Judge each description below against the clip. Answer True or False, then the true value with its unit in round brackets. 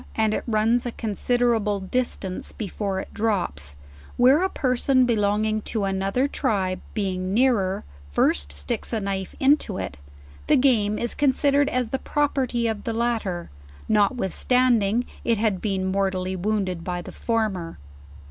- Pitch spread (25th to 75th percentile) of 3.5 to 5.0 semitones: True (4.3 semitones)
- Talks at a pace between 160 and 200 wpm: False (140 wpm)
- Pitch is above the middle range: True (215 Hz)